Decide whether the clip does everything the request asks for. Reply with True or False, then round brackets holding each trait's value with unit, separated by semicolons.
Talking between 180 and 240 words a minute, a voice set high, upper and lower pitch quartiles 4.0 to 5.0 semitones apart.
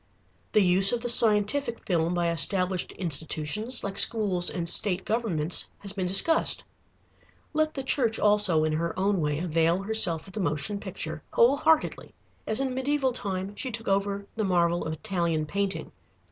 False (165 wpm; 195 Hz; 4.6 semitones)